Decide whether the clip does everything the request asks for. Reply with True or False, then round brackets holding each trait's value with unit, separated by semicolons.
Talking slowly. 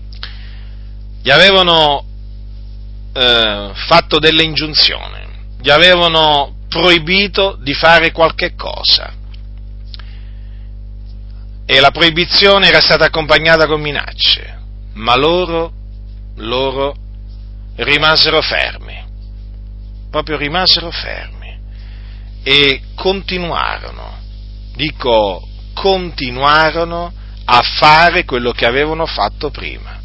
True (80 wpm)